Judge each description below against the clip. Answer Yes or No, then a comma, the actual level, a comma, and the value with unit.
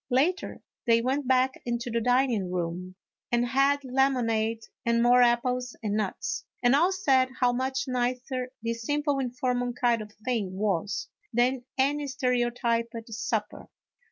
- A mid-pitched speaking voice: No, high, 245 Hz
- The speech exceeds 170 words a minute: No, average, 140 wpm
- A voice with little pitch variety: Yes, narrow, 2.3 semitones